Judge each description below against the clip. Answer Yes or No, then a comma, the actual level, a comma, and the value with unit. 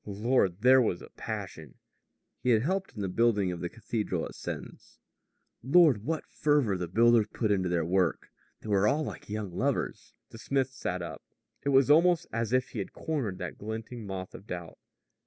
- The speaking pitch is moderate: No, low, 110 Hz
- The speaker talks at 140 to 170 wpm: No, average, 190 wpm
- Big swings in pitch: Yes, wide, 5.7 semitones